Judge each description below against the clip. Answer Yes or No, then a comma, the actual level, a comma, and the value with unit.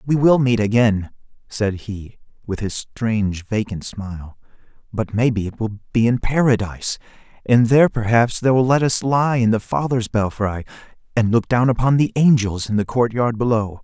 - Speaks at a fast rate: No, average, 180 wpm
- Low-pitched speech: Yes, low, 115 Hz